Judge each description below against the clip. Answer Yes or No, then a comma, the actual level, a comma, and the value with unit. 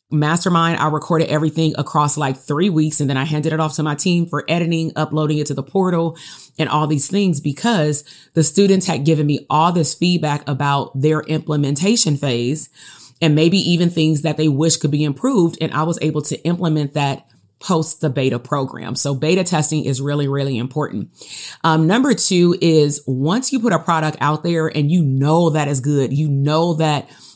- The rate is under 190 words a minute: No, average, 195 wpm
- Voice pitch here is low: No, medium, 155 Hz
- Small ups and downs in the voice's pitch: Yes, narrow, 2.3 semitones